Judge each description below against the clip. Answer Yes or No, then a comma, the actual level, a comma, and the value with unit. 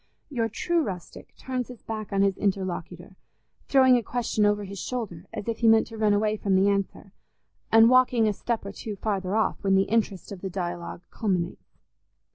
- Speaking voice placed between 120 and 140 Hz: No, high, 205 Hz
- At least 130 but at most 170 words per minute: No, average, 195 wpm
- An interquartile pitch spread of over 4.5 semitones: No, average, 2.9 semitones